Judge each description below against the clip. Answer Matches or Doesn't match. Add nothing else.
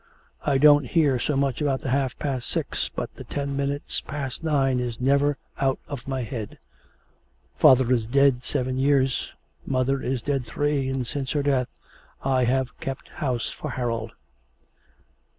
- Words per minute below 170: Matches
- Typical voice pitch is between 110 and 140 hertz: Matches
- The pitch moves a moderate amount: Doesn't match